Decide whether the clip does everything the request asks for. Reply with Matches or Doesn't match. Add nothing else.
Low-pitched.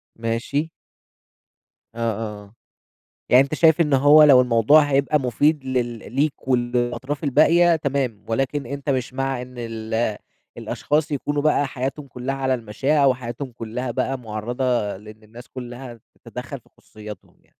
Matches